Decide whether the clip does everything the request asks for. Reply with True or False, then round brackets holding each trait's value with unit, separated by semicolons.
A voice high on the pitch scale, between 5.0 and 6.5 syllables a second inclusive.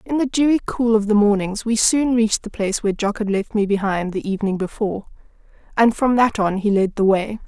True (215 Hz; 6.0 syllables/s)